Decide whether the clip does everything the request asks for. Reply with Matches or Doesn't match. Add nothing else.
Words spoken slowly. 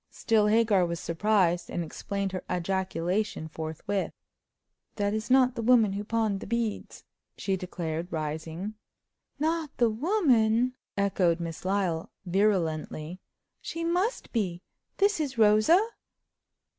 Matches